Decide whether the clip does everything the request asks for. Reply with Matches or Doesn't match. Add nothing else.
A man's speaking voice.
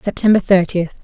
Doesn't match